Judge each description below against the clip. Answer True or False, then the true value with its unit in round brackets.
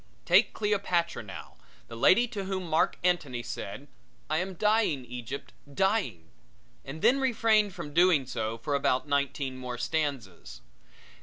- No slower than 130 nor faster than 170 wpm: True (140 wpm)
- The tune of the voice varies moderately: False (7.3 semitones)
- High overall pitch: False (150 Hz)